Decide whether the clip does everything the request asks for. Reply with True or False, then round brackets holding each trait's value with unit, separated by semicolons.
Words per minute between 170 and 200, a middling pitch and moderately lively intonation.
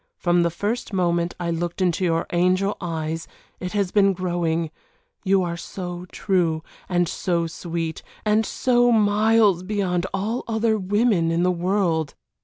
False (150 wpm; 180 Hz; 3.2 semitones)